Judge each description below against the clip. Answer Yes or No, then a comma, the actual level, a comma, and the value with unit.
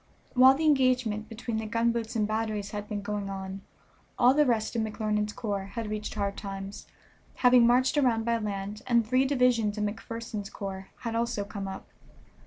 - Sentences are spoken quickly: No, average, 180 wpm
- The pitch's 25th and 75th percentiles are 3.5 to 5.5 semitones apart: No, narrow, 2.6 semitones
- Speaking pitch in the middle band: No, high, 220 Hz